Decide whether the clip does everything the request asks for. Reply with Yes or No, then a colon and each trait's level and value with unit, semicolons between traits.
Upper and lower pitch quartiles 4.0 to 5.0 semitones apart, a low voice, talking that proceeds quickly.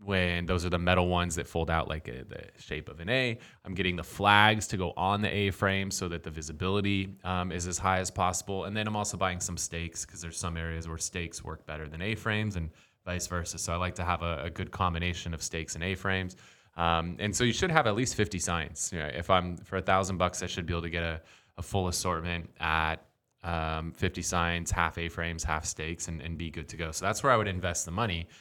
No: narrow, 2.5 semitones; very low, 90 Hz; fast, 260 wpm